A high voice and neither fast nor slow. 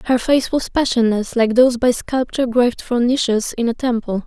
Yes: high, 240 Hz; average, 195 wpm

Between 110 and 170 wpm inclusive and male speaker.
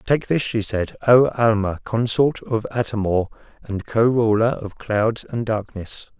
Yes: average, 165 wpm; male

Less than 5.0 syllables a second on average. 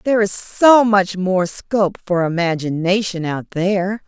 Yes: 4.5 syllables/s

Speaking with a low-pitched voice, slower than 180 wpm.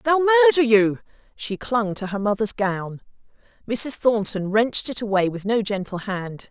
No: high, 220 Hz; average, 165 wpm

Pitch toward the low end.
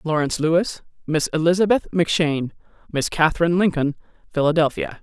No: medium, 160 Hz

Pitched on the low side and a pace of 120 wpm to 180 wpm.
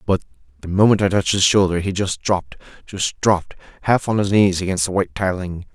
No: very low, 95 Hz; average, 200 wpm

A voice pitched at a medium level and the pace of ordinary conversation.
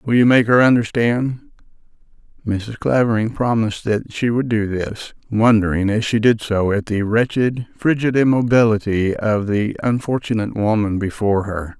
No: low, 110 Hz; average, 150 wpm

